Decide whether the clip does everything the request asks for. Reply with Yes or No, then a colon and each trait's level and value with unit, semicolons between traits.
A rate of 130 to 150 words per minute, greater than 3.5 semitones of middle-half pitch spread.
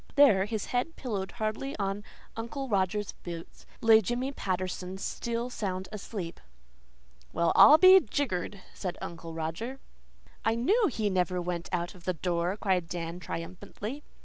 Yes: average, 145 wpm; average, 4.7 semitones